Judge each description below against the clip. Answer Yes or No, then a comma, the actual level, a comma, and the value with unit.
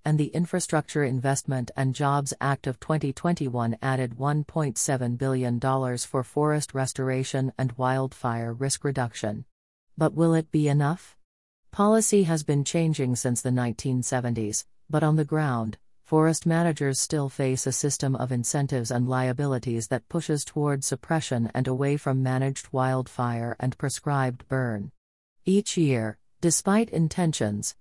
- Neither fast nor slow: No, slow, 130 wpm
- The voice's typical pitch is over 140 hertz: No, low, 135 Hz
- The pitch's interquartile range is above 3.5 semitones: No, average, 3.1 semitones